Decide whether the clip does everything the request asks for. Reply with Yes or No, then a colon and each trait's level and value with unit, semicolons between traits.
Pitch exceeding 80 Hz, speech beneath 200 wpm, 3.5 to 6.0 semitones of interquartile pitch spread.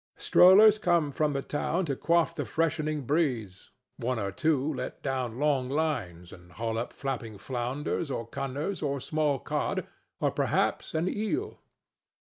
Yes: medium, 140 Hz; average, 150 wpm; average, 4.7 semitones